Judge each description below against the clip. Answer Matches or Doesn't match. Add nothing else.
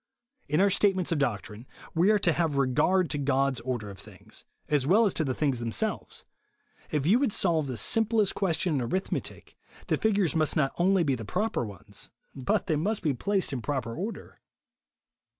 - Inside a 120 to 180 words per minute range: Doesn't match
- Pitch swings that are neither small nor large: Doesn't match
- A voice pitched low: Doesn't match